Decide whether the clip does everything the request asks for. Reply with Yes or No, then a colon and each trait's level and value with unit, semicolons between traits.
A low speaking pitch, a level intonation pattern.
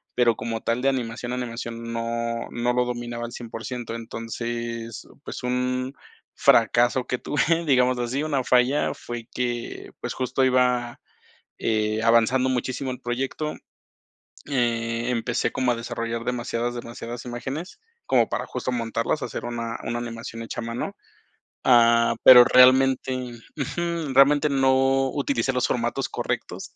Yes: low, 120 Hz; narrow, 1.9 semitones